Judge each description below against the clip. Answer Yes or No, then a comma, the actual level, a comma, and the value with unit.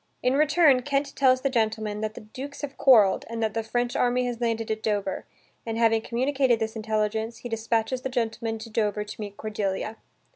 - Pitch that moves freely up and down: No, narrow, 2.5 semitones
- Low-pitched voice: No, high, 225 Hz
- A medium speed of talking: Yes, average, 195 wpm